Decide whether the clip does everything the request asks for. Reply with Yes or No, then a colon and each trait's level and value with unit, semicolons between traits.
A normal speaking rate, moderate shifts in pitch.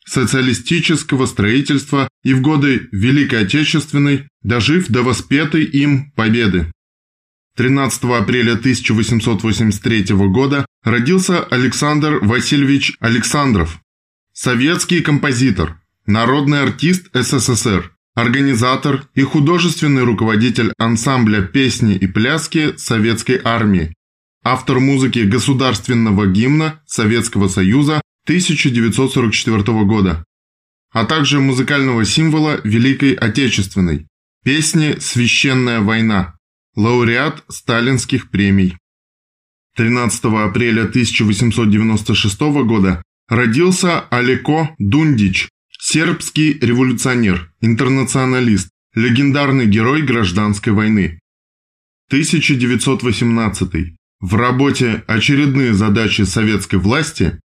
No: slow, 80 wpm; average, 4.9 semitones